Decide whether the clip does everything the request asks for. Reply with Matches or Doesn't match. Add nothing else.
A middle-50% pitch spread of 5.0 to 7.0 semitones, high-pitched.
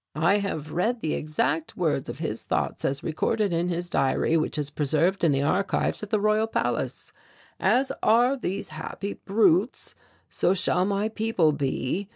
Doesn't match